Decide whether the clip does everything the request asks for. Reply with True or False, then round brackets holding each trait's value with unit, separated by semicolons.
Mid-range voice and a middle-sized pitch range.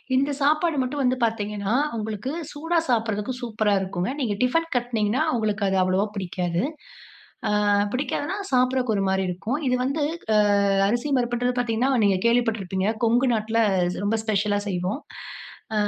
False (225 Hz; 3.7 semitones)